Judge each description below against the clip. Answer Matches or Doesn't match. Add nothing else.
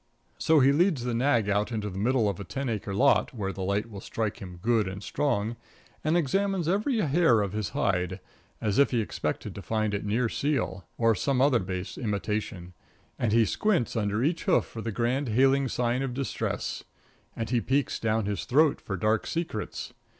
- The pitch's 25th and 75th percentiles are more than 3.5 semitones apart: Matches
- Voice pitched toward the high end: Doesn't match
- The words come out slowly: Doesn't match